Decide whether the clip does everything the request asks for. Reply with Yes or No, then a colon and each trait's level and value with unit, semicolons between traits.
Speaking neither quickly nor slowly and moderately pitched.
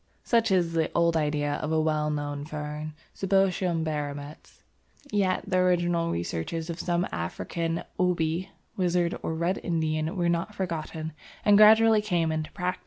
Yes: average, 150 wpm; medium, 165 Hz